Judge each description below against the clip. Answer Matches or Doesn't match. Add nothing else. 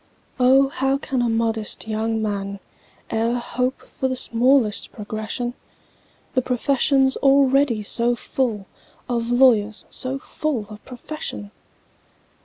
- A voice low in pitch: Doesn't match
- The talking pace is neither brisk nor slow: Doesn't match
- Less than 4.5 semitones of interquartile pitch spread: Matches